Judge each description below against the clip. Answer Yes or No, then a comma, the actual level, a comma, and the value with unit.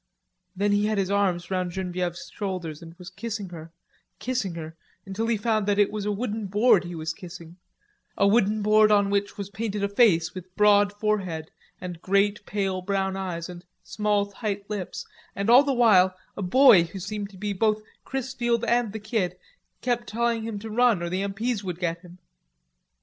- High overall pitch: Yes, high, 200 Hz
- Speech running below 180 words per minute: No, average, 190 wpm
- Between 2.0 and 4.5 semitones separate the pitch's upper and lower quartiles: Yes, average, 2.8 semitones